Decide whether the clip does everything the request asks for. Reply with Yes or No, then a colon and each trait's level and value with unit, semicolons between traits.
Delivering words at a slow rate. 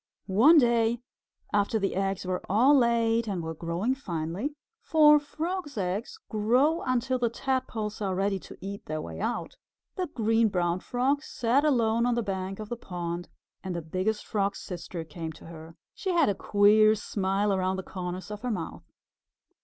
No: average, 175 wpm